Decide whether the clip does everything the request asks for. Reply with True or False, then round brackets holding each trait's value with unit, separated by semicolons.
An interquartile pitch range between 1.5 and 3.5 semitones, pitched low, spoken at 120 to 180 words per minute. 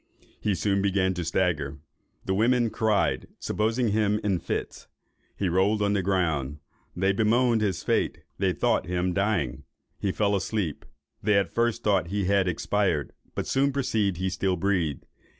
True (2.9 semitones; 100 Hz; 160 wpm)